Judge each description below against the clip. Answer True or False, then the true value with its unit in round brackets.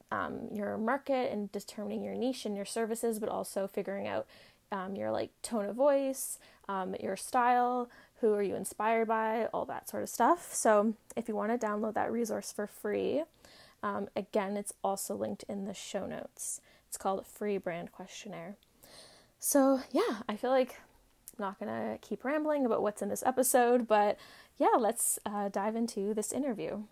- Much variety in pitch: False (3.5 semitones)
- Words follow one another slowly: False (180 wpm)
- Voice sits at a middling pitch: False (215 Hz)